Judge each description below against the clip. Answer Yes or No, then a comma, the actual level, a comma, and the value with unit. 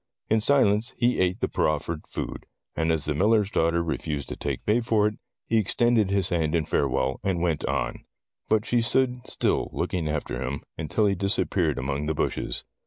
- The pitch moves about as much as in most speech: No, wide, 5.9 semitones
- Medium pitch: No, very low, 90 Hz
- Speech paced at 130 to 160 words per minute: No, average, 185 wpm